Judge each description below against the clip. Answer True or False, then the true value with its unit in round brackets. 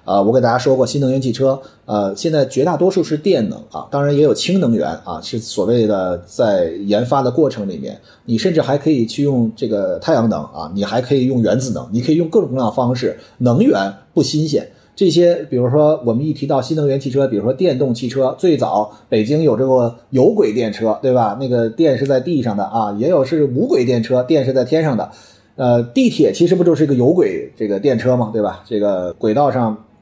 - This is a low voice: True (130 Hz)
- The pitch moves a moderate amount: True (4.6 semitones)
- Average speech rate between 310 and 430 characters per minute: True (325 characters per minute)